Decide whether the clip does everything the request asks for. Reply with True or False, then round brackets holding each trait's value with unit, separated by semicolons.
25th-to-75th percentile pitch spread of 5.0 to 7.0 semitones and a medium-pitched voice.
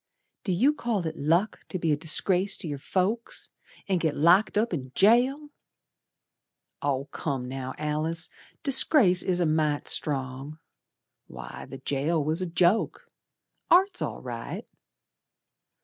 True (5.3 semitones; 170 Hz)